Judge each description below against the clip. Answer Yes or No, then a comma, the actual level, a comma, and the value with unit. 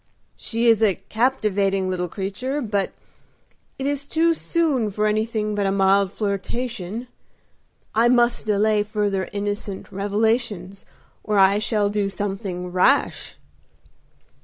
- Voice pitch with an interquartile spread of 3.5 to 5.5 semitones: No, average, 3.0 semitones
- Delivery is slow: Yes, slow, 120 wpm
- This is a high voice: Yes, high, 210 Hz